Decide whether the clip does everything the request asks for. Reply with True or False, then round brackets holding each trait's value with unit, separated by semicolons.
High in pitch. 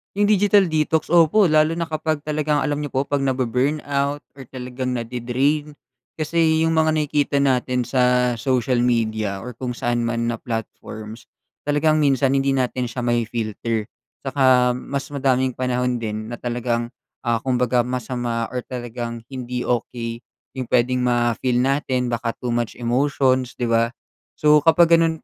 False (125 Hz)